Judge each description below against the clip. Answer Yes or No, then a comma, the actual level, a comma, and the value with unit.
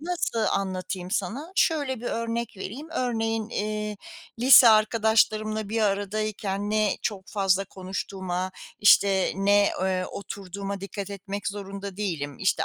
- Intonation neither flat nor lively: No, narrow, 2.3 semitones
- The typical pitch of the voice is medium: No, high, 205 Hz